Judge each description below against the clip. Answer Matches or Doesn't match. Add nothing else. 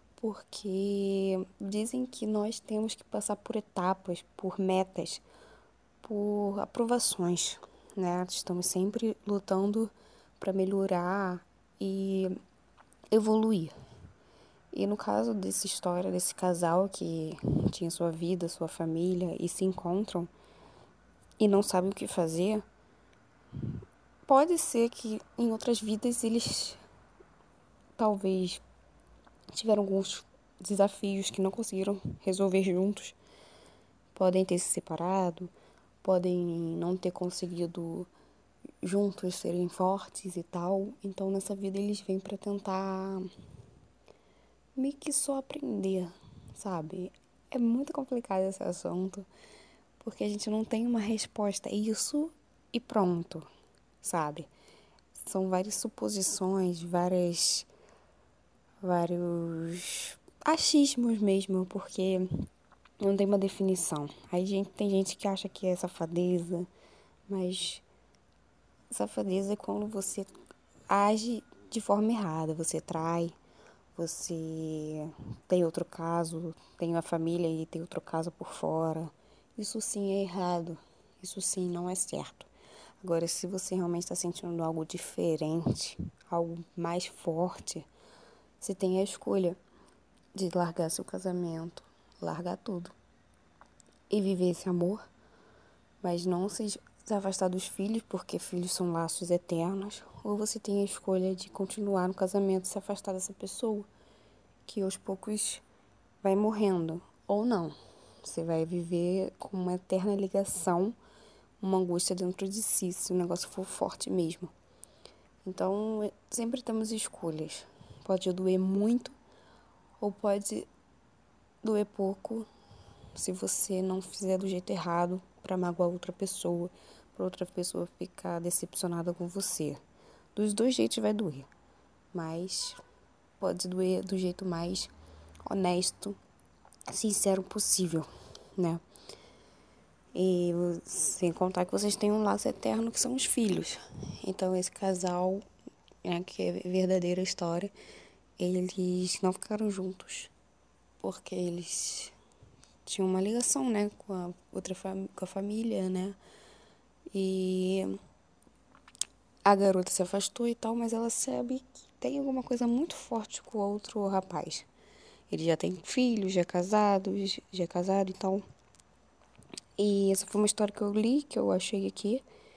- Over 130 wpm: Doesn't match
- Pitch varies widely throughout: Doesn't match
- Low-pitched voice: Doesn't match